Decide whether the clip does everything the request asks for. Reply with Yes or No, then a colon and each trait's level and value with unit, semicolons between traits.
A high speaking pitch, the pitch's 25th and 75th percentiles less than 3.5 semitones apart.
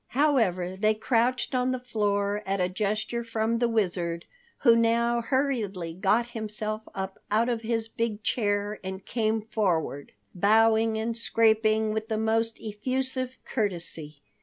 Yes: high, 220 Hz; narrow, 2.4 semitones